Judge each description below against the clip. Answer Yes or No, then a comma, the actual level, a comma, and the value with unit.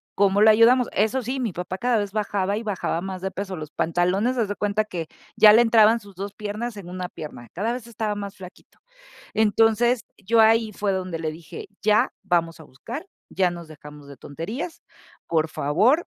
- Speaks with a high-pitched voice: Yes, high, 205 Hz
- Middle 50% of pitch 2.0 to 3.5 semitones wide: No, average, 4.0 semitones